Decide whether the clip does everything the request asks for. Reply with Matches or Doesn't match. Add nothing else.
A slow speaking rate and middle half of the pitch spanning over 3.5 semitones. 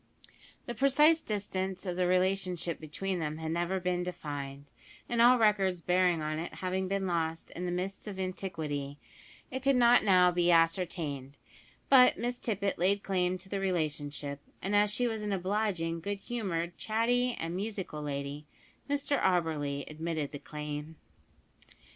Doesn't match